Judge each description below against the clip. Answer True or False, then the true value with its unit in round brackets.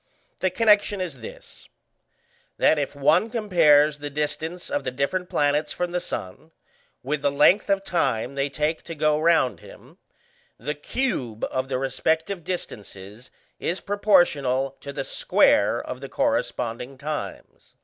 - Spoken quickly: False (145 wpm)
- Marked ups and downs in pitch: False (4.6 semitones)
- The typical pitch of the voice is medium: True (150 Hz)